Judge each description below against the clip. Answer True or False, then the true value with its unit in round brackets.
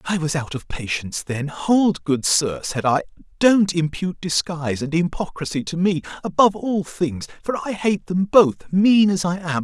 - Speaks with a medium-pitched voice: True (170 Hz)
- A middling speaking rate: True (185 wpm)